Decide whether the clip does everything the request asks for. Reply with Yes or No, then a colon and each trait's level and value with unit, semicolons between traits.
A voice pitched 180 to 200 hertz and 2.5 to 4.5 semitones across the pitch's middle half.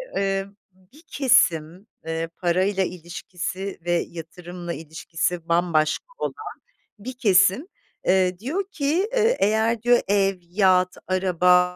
Yes: medium, 185 Hz; average, 3.4 semitones